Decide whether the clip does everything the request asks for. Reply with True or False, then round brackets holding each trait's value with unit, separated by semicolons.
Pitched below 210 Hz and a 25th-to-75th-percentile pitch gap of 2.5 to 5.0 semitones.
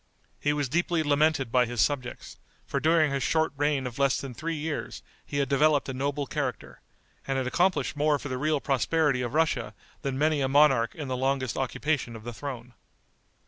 True (140 Hz; 2.8 semitones)